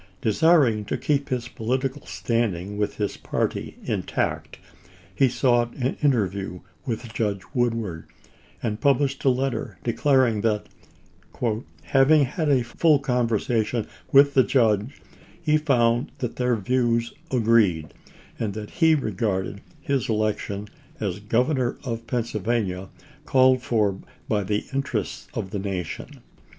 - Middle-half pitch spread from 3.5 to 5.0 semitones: Yes, average, 3.9 semitones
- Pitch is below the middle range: Yes, low, 115 Hz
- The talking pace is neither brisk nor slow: No, slow, 125 wpm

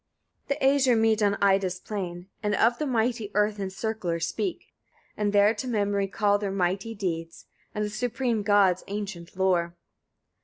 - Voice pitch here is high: Yes, high, 205 Hz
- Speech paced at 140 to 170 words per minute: Yes, average, 160 wpm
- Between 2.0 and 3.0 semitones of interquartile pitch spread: Yes, average, 2.7 semitones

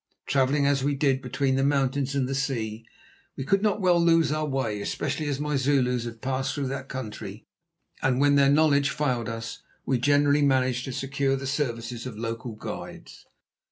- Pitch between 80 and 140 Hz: Yes, low, 135 Hz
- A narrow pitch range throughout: Yes, narrow, 2.2 semitones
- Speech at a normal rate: Yes, average, 185 wpm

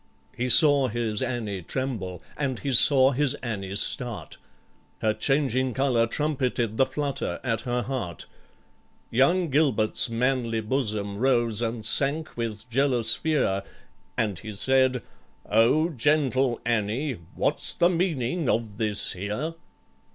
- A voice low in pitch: Yes, low, 125 Hz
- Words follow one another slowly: Yes, slow, 125 wpm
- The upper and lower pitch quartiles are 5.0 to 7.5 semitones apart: No, average, 3.6 semitones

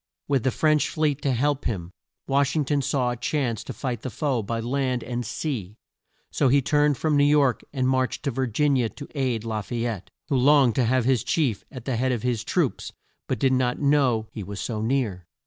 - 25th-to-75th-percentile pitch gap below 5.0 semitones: Yes, average, 3.5 semitones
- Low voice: Yes, low, 130 Hz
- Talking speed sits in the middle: No, fast, 230 wpm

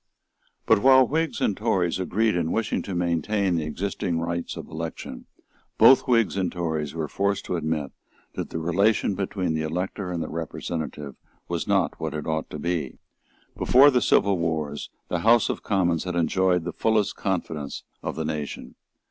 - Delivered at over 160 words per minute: Yes, average, 175 wpm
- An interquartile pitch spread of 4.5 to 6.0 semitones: No, average, 4.0 semitones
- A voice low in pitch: Yes, very low, 85 Hz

